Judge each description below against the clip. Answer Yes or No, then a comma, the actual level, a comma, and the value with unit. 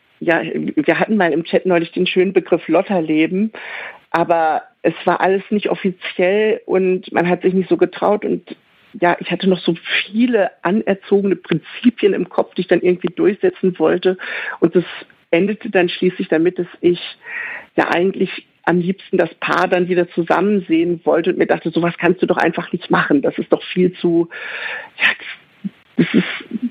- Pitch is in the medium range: Yes, medium, 180 Hz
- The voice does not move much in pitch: Yes, narrow, 2.3 semitones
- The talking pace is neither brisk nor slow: Yes, average, 180 wpm